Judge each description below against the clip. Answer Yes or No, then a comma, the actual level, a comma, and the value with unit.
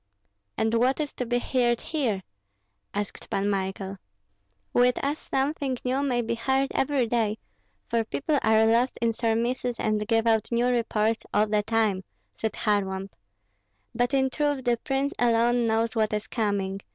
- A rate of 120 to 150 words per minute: No, average, 160 wpm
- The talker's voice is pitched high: Yes, high, 230 Hz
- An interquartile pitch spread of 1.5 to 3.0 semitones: Yes, average, 2.7 semitones